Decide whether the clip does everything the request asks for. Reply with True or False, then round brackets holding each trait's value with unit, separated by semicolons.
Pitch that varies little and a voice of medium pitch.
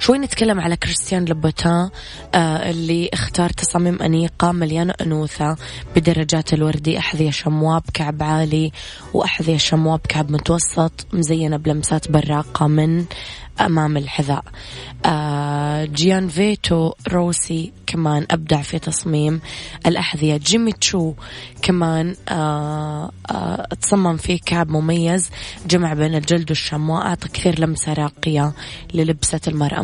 True (2.1 semitones; 160 Hz)